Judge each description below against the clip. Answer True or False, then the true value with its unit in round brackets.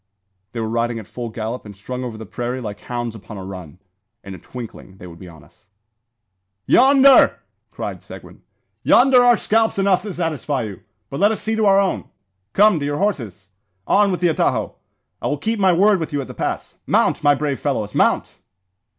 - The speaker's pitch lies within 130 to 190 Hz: True (135 Hz)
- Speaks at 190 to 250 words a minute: True (200 wpm)